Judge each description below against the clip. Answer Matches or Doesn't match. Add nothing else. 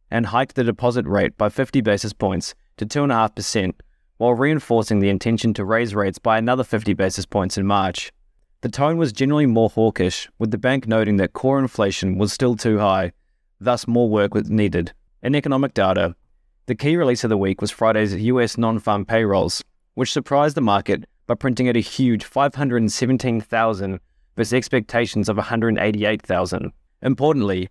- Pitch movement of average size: Matches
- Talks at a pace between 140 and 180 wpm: Matches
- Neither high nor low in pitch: Doesn't match